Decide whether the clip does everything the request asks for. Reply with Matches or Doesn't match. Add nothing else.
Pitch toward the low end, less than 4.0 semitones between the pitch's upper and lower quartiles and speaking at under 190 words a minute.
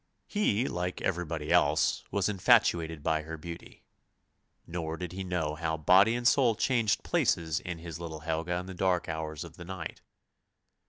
Matches